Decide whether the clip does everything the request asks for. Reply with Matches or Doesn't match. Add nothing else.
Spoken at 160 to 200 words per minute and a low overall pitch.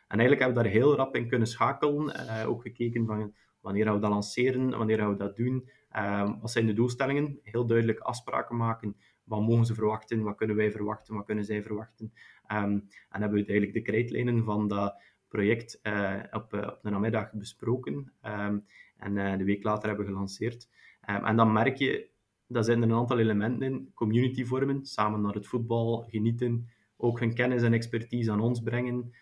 Matches